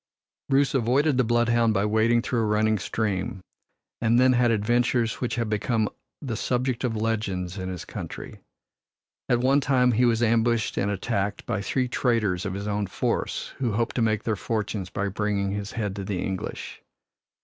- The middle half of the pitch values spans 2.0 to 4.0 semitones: Yes, average, 2.8 semitones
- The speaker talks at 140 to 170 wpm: No, average, 180 wpm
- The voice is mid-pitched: No, low, 110 Hz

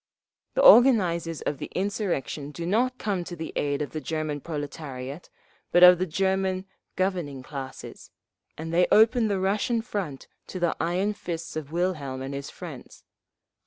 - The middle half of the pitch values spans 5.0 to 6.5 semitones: No, average, 4.6 semitones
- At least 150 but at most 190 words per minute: Yes, average, 160 wpm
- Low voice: No, medium, 175 Hz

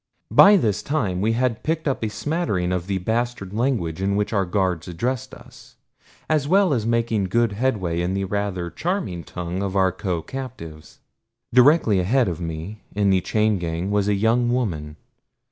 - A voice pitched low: Yes, low, 100 Hz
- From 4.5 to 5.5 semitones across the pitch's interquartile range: Yes, average, 5.1 semitones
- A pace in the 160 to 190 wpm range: Yes, average, 180 wpm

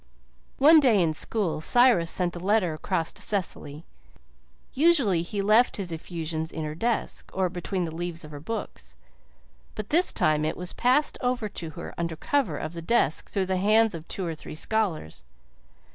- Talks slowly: No, average, 180 wpm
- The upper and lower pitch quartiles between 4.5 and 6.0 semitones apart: Yes, average, 5.3 semitones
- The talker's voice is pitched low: No, medium, 180 Hz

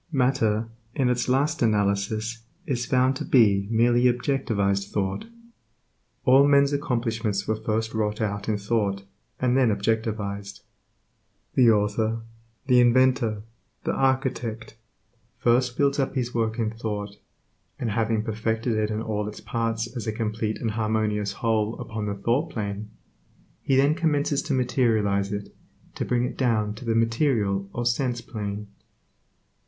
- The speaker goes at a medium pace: Yes, average, 145 wpm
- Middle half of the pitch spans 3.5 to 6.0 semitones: No, average, 2.9 semitones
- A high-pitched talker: No, low, 115 Hz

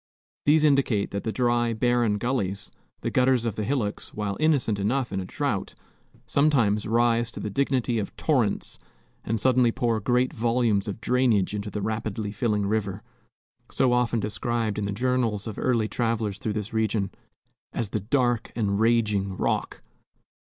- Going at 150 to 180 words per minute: Yes, average, 160 wpm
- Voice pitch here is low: Yes, low, 115 Hz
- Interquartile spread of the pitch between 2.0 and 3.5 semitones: Yes, average, 2.9 semitones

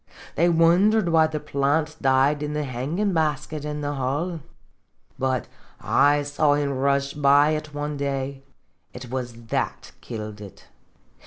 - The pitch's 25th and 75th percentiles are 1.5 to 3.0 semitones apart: Yes, narrow, 2.4 semitones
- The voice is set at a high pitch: No, medium, 145 Hz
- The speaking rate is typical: Yes, average, 155 wpm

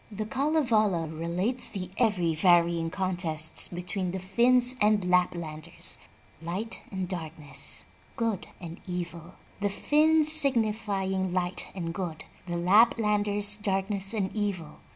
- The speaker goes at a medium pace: No, slow, 125 wpm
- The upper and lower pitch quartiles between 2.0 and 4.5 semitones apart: Yes, average, 3.8 semitones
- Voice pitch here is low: No, high, 190 Hz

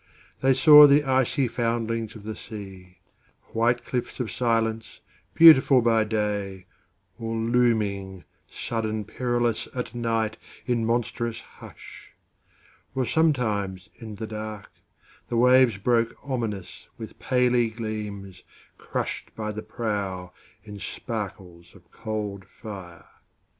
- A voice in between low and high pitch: No, low, 110 Hz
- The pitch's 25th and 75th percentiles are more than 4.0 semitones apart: No, average, 2.9 semitones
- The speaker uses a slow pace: Yes, slow, 100 wpm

